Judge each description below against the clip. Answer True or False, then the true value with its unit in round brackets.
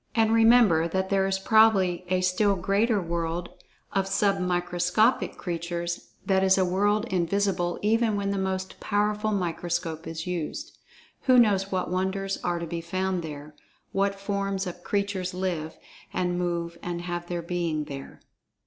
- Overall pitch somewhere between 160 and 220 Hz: True (185 Hz)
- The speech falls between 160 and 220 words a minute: False (150 wpm)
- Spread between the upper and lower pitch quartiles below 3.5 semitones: True (2.4 semitones)